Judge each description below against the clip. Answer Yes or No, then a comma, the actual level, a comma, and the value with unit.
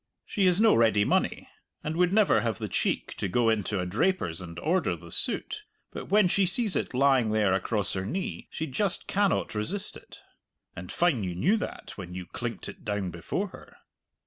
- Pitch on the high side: No, low, 115 Hz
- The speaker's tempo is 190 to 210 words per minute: Yes, average, 200 wpm